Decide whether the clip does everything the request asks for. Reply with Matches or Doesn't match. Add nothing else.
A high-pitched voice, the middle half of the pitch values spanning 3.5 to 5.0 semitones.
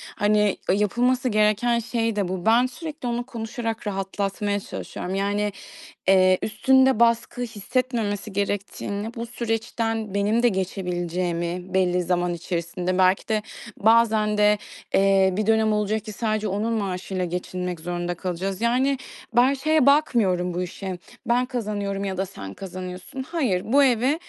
Matches